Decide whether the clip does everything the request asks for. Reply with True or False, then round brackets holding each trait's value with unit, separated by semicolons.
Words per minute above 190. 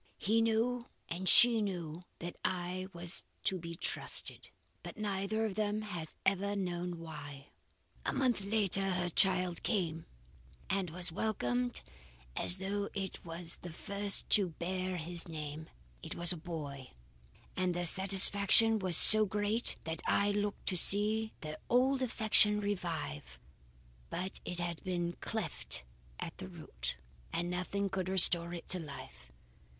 False (145 wpm)